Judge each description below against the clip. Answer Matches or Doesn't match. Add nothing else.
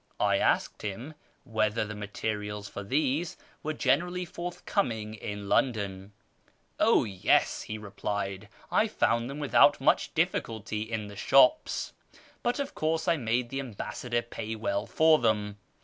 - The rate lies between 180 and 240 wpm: Doesn't match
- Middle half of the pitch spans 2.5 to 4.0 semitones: Doesn't match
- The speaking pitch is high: Doesn't match